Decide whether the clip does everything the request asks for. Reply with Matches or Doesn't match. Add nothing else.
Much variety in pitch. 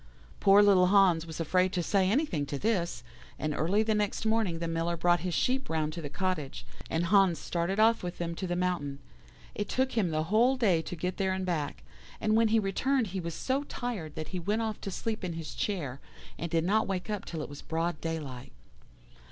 Doesn't match